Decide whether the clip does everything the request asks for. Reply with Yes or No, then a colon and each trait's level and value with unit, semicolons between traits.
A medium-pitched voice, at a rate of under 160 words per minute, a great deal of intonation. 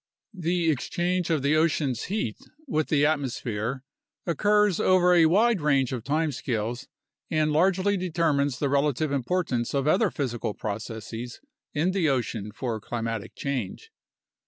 Yes: medium, 145 Hz; slow, 135 wpm; wide, 6.1 semitones